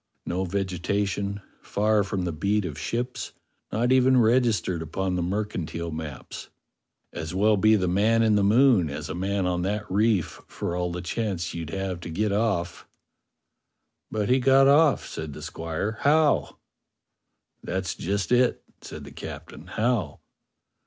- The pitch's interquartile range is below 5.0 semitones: Yes, average, 4.0 semitones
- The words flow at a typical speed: Yes, average, 160 wpm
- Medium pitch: No, low, 100 Hz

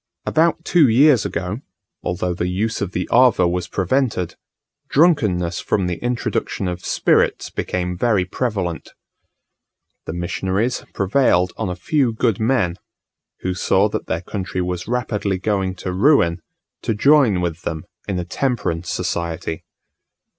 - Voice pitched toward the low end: Yes, very low, 95 Hz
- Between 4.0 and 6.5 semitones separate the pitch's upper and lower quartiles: Yes, average, 5.2 semitones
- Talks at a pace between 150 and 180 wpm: No, average, 140 wpm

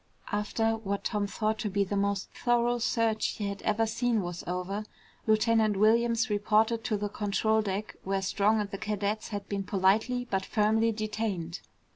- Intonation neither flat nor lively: No, narrow, 1.9 semitones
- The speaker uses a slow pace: No, average, 170 wpm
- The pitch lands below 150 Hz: No, high, 215 Hz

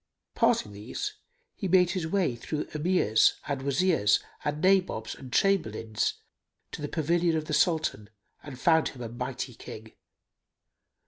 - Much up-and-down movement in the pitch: Yes, wide, 6.6 semitones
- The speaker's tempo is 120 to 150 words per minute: Yes, average, 140 wpm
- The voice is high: No, medium, 150 Hz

